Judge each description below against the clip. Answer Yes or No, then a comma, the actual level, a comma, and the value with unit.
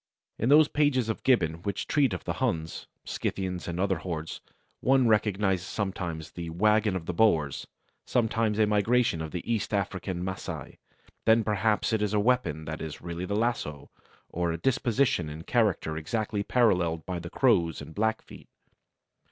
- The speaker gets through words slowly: No, average, 165 wpm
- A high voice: No, low, 100 Hz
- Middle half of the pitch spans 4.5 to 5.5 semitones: Yes, average, 4.9 semitones